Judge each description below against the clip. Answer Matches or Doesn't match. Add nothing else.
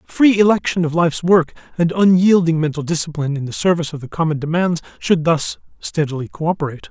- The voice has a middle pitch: Matches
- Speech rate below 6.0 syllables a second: Doesn't match